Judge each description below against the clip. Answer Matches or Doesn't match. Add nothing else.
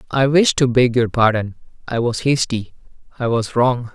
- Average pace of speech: Matches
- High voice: Doesn't match